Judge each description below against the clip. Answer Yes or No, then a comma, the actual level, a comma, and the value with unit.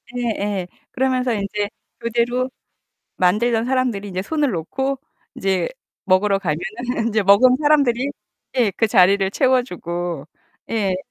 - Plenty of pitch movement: No, average, 4.6 semitones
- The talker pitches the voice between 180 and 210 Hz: No, high, 220 Hz